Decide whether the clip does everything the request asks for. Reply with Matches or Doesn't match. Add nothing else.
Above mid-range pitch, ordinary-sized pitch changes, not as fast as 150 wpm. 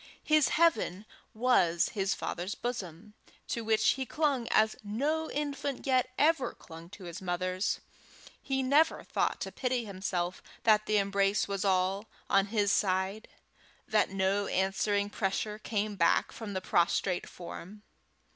Matches